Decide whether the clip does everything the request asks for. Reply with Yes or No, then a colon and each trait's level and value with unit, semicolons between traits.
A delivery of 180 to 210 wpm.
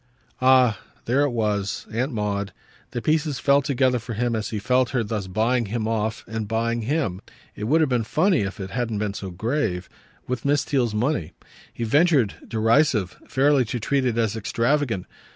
Yes: average, 185 wpm